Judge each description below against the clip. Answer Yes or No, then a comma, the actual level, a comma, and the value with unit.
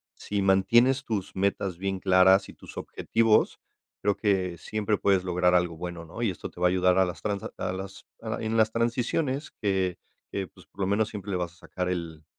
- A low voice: Yes, very low, 95 Hz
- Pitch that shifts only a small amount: No, average, 3.0 semitones